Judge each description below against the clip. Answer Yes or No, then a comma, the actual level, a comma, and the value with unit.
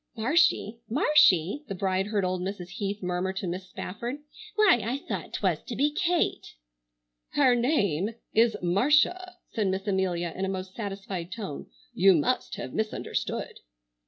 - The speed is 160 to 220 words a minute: No, average, 150 wpm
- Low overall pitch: No, high, 200 Hz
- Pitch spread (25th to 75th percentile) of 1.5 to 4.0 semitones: No, average, 5.1 semitones